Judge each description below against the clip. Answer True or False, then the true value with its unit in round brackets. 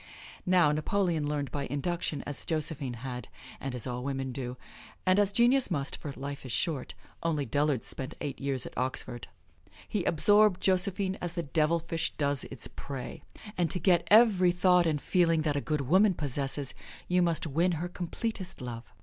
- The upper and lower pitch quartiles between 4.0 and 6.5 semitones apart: True (4.7 semitones)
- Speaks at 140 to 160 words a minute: False (175 wpm)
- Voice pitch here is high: False (155 Hz)